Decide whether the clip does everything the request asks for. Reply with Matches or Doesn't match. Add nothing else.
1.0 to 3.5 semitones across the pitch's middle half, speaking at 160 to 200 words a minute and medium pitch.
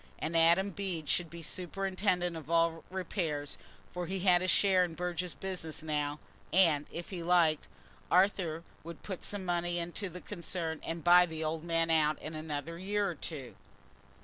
Matches